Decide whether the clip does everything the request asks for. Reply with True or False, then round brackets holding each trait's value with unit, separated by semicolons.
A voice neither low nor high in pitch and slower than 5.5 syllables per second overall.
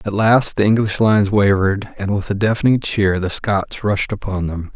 False (100 Hz; 5.0 syllables/s)